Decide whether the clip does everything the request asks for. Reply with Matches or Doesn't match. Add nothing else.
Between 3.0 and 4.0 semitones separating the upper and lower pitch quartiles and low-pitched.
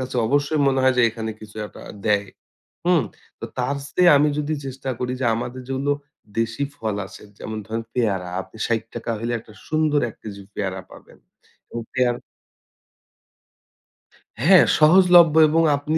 Doesn't match